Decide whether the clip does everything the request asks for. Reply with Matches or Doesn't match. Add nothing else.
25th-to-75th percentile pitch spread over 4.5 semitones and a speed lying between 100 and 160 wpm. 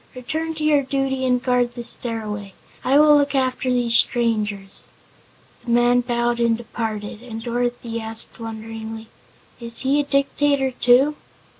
Doesn't match